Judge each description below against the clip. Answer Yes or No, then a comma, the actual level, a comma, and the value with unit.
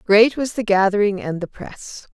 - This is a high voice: Yes, high, 205 Hz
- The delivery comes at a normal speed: Yes, average, 195 wpm